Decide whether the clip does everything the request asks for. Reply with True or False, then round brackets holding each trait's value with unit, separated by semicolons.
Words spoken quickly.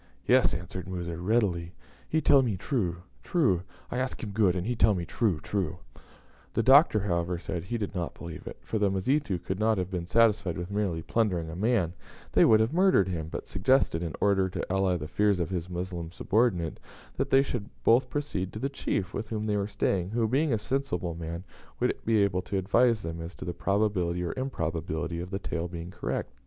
True (210 wpm)